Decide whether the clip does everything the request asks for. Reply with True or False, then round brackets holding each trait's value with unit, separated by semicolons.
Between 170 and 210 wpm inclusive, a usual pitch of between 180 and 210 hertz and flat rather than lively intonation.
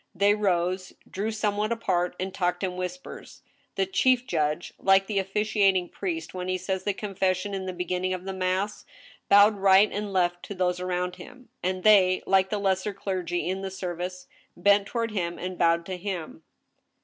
True (180 wpm; 190 Hz; 2.0 semitones)